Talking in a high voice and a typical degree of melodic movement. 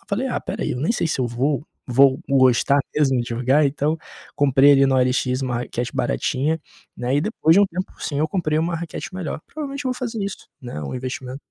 No: medium, 140 Hz; average, 4.6 semitones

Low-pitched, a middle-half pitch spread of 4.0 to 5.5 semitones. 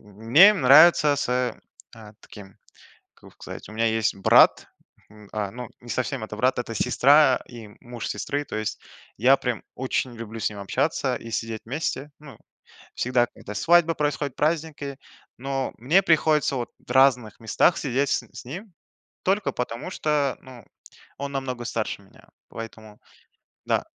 Yes: low, 125 Hz; average, 4.3 semitones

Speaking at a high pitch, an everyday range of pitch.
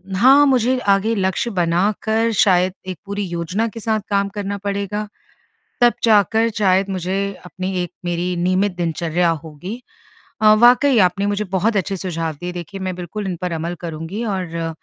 Yes: high, 195 Hz; average, 3.2 semitones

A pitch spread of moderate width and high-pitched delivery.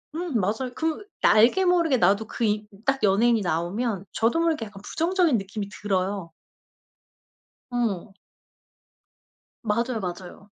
Yes: average, 4.8 semitones; high, 220 Hz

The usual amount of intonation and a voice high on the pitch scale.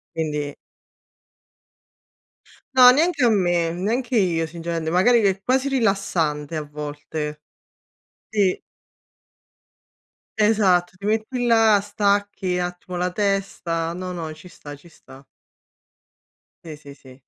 No: average, 4.7 semitones; medium, 180 Hz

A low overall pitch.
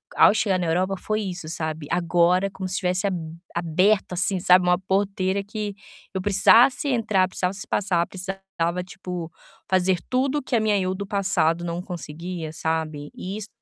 No: medium, 185 Hz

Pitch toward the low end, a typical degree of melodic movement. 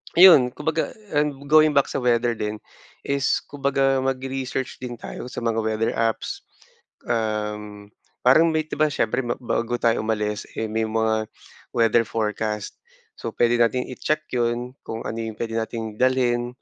Yes: low, 120 Hz; average, 3.1 semitones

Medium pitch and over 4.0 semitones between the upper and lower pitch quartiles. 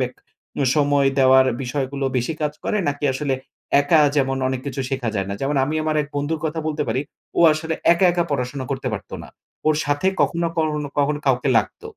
No: medium, 145 Hz; narrow, 2.5 semitones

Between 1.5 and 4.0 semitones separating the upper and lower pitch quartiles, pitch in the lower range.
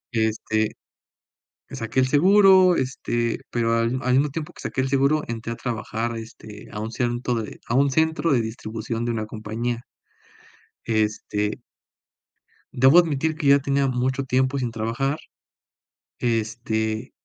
Yes: average, 3.4 semitones; low, 120 Hz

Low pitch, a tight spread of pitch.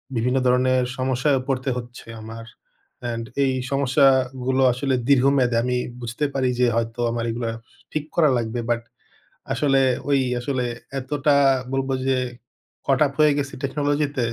Yes: low, 130 Hz; narrow, 2.2 semitones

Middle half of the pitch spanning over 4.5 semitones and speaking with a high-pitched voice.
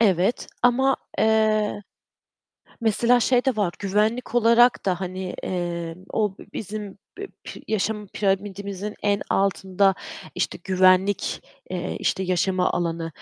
No: average, 2.9 semitones; high, 200 Hz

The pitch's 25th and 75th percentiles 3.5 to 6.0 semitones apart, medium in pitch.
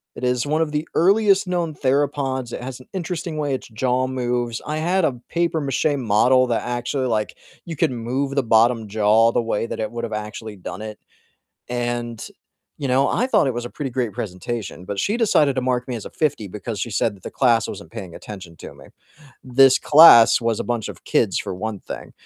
No: average, 4.2 semitones; low, 125 Hz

